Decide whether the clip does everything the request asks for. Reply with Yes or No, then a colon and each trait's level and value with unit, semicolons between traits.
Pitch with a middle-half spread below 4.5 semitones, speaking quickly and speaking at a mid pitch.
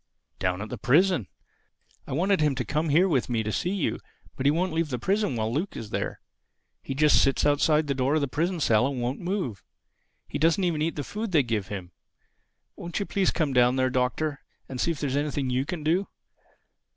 No: average, 5.0 semitones; fast, 225 wpm; medium, 145 Hz